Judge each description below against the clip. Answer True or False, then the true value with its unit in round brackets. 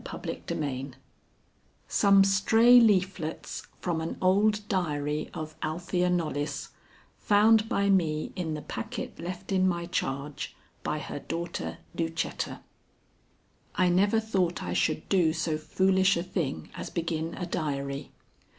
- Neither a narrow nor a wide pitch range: True (3.8 semitones)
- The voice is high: False (175 Hz)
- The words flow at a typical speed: False (125 wpm)